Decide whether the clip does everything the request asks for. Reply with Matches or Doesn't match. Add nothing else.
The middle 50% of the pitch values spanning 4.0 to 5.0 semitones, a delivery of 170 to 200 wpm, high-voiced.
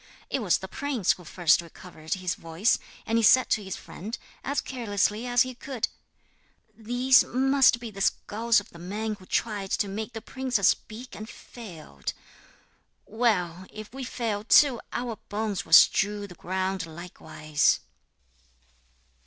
Doesn't match